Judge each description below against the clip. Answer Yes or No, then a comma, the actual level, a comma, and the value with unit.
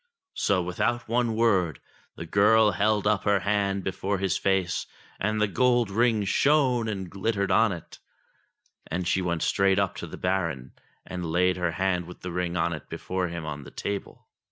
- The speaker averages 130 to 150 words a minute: No, average, 180 wpm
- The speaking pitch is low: Yes, very low, 95 Hz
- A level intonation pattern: No, average, 3.2 semitones